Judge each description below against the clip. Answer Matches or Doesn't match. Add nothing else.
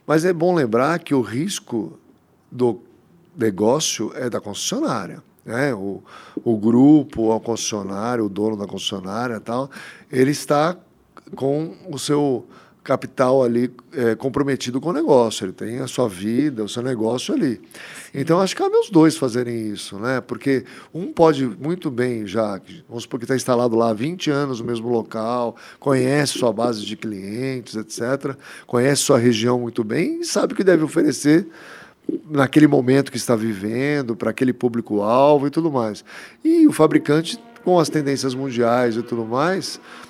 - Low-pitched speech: Matches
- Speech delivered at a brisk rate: Doesn't match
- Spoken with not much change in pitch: Doesn't match